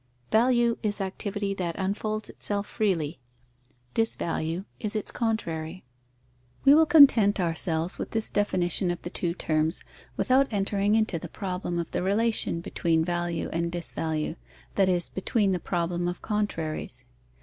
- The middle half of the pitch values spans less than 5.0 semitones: Yes, average, 3.9 semitones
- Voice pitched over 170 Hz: Yes, high, 190 Hz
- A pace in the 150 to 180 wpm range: No, average, 140 wpm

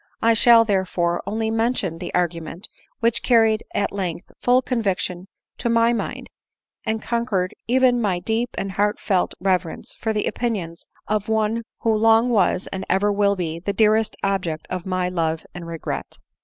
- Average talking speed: Yes, average, 160 wpm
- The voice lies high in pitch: Yes, high, 205 Hz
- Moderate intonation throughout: Yes, average, 3.8 semitones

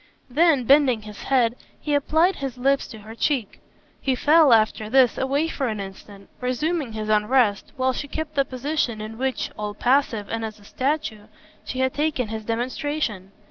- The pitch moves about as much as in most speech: Yes, average, 4.6 semitones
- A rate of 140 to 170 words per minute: No, average, 180 wpm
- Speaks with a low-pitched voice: No, very high, 255 Hz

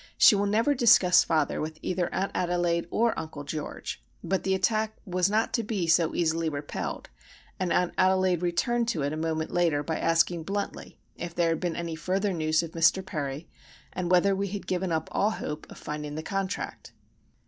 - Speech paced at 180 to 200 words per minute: Yes, average, 190 wpm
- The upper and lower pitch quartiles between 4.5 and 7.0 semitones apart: No, average, 3.3 semitones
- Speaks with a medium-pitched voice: Yes, medium, 175 Hz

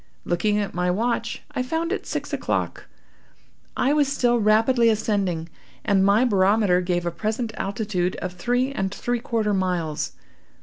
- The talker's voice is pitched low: No, high, 210 Hz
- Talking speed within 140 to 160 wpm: Yes, average, 150 wpm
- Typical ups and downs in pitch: Yes, average, 4.8 semitones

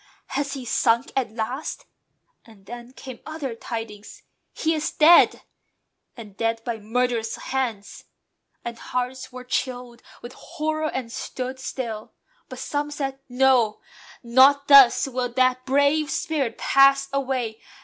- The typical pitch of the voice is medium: No, very high, 255 Hz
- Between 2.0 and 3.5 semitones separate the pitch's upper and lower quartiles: Yes, average, 2.8 semitones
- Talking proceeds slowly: Yes, slow, 130 wpm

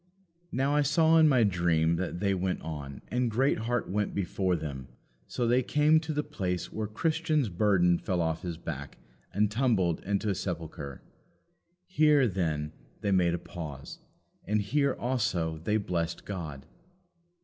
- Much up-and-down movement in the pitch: Yes, wide, 6.8 semitones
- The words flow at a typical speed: Yes, average, 155 wpm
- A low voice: Yes, very low, 95 Hz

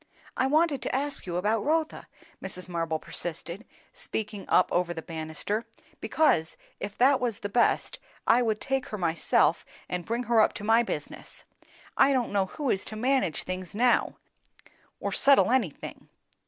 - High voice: Yes, high, 215 Hz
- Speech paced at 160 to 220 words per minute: Yes, average, 165 wpm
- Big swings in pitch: Yes, wide, 6.2 semitones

